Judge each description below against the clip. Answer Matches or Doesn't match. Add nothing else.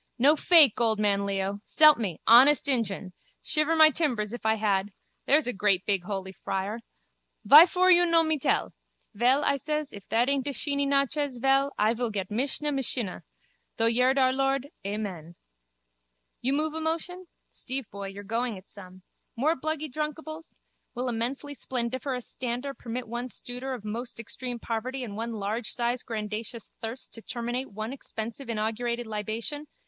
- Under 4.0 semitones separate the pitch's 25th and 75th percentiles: Doesn't match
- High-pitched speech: Matches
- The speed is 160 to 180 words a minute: Matches